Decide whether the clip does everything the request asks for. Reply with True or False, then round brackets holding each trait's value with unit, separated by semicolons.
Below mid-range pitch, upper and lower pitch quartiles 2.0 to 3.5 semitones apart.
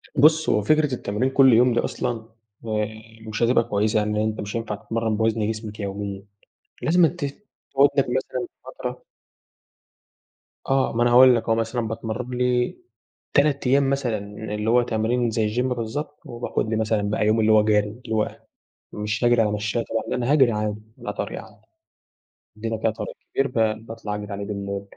True (115 Hz; 2.7 semitones)